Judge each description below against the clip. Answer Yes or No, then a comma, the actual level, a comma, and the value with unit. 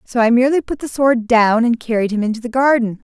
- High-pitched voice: Yes, high, 240 Hz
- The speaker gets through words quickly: Yes, fast, 250 wpm